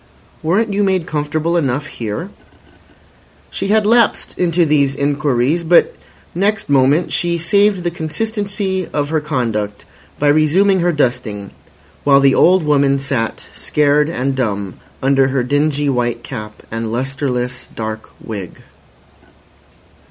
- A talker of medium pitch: Yes, medium, 145 Hz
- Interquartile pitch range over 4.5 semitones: Yes, average, 5.3 semitones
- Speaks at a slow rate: Yes, slow, 130 wpm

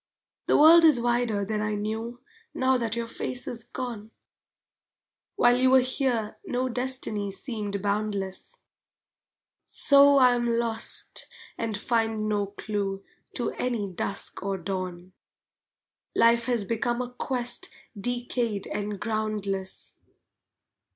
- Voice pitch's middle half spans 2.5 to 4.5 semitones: Yes, average, 3.2 semitones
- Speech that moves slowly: Yes, slow, 120 wpm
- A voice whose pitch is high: Yes, high, 225 Hz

